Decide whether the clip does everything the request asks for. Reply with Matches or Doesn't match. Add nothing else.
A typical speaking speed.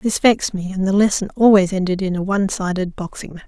Doesn't match